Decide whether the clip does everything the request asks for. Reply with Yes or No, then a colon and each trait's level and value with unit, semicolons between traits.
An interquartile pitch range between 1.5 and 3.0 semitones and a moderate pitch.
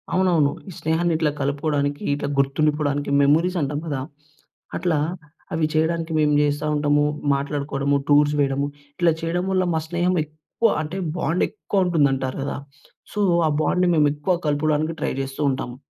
Yes: average, 2.7 semitones; medium, 150 Hz